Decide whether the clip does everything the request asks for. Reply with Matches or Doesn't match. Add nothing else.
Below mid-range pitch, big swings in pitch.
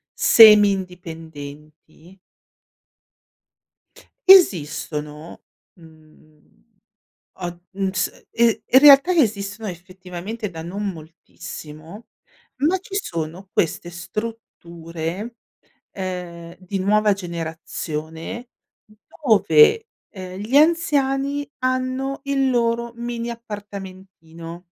Doesn't match